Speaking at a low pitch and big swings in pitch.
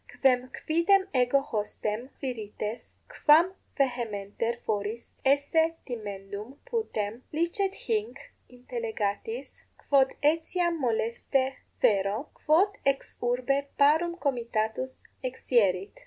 No: very high, 255 Hz; wide, 5.9 semitones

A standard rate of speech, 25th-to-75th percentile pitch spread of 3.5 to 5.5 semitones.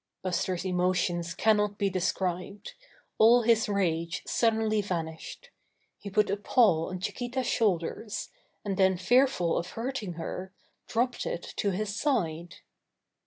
No: slow, 125 wpm; average, 3.9 semitones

